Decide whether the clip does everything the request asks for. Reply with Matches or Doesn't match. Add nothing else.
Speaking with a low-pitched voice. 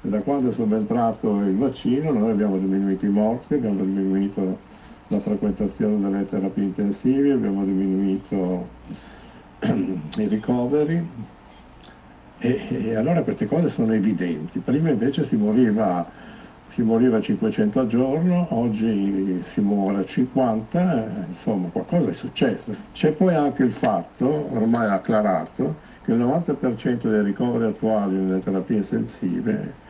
Matches